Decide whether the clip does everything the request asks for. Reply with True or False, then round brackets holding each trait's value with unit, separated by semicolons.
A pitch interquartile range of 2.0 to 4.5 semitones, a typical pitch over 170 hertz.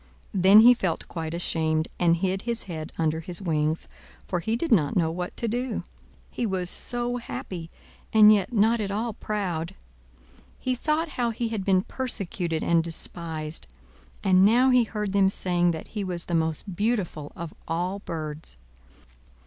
False (5.0 semitones; 185 Hz)